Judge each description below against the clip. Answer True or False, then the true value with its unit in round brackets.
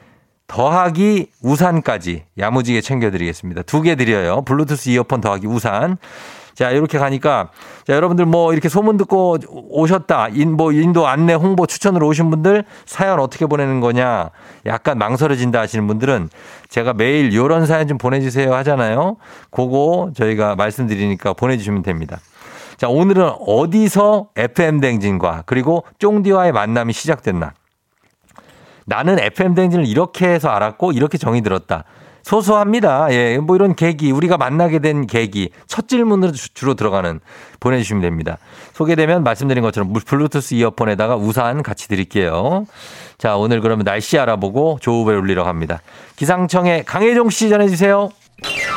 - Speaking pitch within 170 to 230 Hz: False (140 Hz)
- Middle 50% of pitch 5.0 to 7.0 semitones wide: False (7.8 semitones)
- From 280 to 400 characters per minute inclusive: True (350 characters per minute)